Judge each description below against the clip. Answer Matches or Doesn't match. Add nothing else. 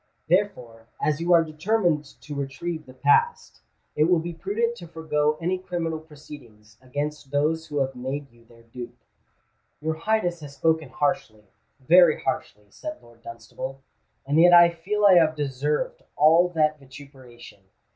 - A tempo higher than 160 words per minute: Doesn't match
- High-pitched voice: Doesn't match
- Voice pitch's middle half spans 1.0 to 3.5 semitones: Doesn't match